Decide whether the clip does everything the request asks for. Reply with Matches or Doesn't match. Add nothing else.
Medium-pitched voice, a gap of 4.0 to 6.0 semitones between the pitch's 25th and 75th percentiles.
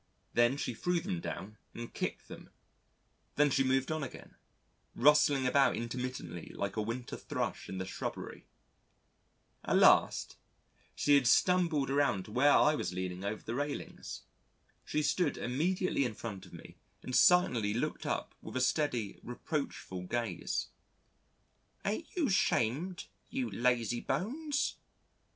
Doesn't match